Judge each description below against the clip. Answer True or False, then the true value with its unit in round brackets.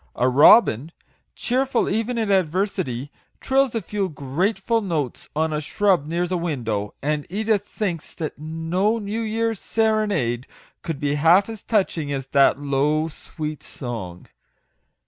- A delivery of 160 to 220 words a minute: False (140 wpm)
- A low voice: False (165 Hz)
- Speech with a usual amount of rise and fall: False (6.5 semitones)